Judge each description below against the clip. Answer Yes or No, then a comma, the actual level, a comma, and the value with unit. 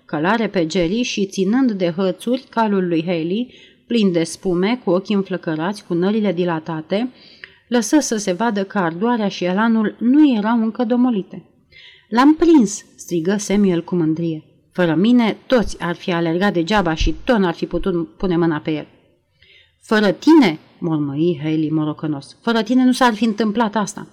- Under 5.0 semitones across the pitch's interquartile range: No, average, 5.3 semitones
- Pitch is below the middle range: No, high, 195 Hz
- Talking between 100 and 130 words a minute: No, average, 165 wpm